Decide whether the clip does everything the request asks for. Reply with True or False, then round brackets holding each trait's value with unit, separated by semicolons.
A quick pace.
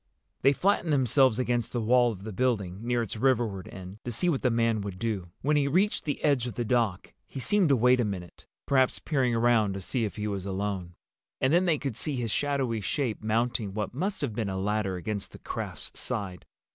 True (220 wpm)